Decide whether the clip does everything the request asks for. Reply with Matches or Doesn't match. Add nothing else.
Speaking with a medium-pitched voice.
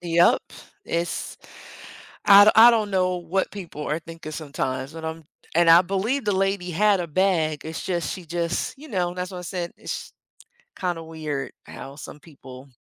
Matches